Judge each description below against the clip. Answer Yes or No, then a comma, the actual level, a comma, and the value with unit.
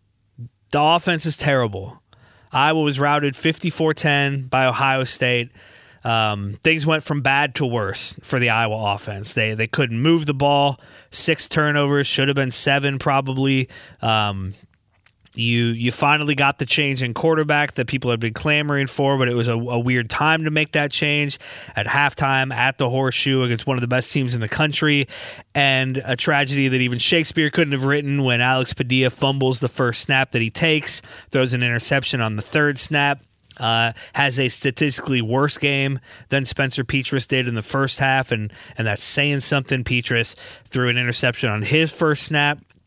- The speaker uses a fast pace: No, average, 180 wpm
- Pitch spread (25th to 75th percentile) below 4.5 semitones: Yes, average, 3.3 semitones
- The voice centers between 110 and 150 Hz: Yes, low, 135 Hz